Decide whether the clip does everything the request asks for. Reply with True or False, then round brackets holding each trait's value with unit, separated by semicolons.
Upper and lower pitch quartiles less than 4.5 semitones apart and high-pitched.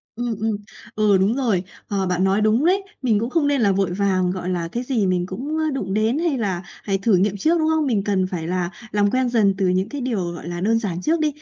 False (5.0 semitones; 205 Hz)